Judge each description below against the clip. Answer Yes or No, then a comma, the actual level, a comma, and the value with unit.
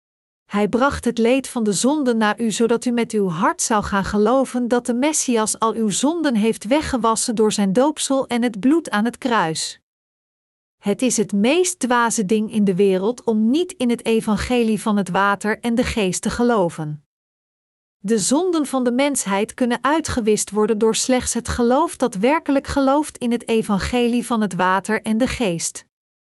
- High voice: Yes, high, 230 Hz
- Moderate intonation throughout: Yes, average, 3.2 semitones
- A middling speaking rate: Yes, average, 180 wpm